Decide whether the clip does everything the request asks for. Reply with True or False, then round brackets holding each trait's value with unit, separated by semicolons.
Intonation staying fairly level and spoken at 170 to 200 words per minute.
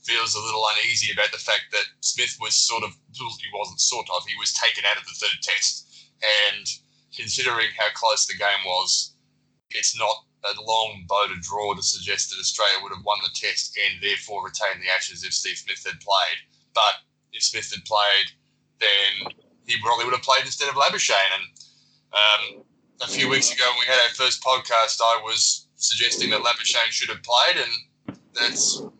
True (2.3 semitones; 190 wpm)